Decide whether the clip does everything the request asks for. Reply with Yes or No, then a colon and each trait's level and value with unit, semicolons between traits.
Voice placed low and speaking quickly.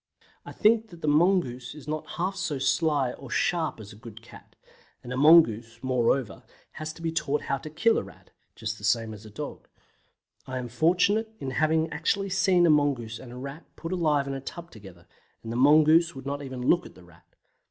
No: medium, 145 Hz; fast, 215 wpm